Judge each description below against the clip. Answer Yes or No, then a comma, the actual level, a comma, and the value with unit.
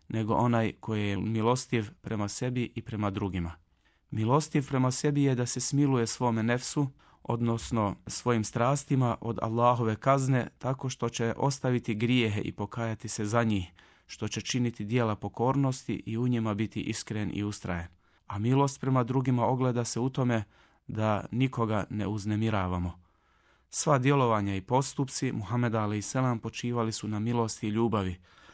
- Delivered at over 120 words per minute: Yes, average, 150 wpm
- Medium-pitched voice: No, low, 115 Hz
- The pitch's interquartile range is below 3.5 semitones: Yes, average, 3.1 semitones